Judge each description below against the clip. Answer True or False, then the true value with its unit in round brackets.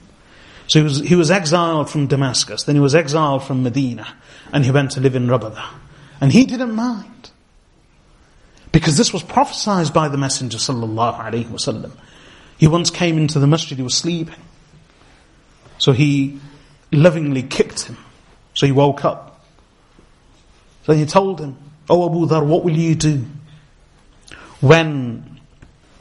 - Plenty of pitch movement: False (3.4 semitones)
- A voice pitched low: False (145 Hz)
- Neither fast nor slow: True (145 wpm)